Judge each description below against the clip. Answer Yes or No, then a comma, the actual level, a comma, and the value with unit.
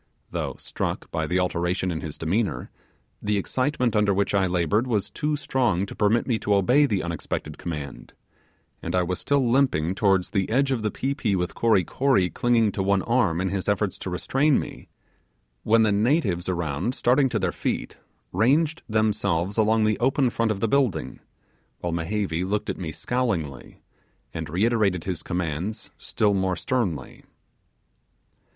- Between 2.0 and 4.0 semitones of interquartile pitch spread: No, average, 4.9 semitones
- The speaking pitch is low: Yes, low, 100 Hz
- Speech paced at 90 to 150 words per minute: No, average, 170 wpm